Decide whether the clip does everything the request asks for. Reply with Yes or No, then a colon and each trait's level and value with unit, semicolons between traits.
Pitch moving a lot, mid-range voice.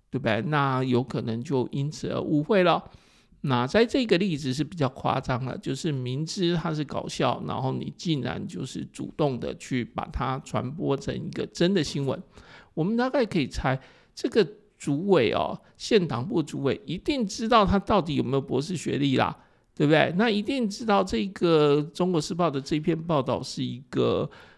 Yes: wide, 6.9 semitones; medium, 155 Hz